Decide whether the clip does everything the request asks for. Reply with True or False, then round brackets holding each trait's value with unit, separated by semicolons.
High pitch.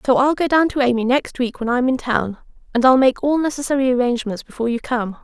True (250 Hz)